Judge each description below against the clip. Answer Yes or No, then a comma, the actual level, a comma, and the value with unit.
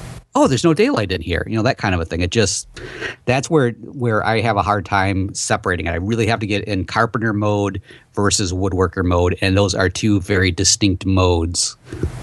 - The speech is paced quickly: Yes, fast, 210 wpm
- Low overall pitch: Yes, low, 100 Hz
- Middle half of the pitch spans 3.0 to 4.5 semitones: Yes, average, 3.3 semitones